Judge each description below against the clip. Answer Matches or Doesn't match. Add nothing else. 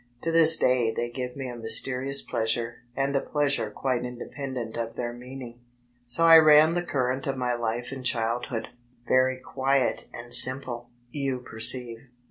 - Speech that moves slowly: Doesn't match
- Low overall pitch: Matches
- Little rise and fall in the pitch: Matches